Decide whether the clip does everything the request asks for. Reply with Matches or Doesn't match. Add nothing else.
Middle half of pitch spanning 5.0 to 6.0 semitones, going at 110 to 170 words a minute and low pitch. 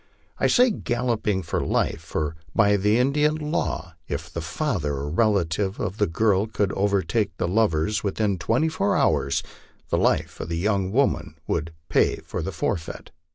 Matches